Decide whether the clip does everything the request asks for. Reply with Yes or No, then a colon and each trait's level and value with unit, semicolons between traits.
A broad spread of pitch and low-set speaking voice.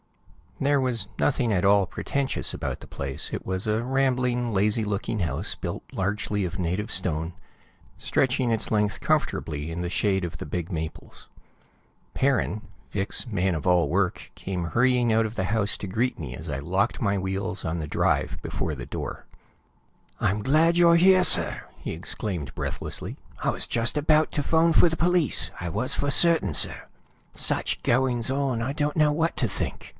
Yes: wide, 6.6 semitones; low, 105 Hz